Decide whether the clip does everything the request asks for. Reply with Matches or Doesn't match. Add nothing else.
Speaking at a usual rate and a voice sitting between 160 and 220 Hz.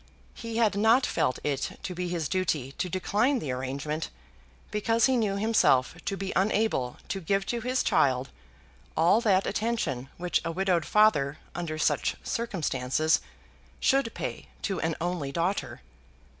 Matches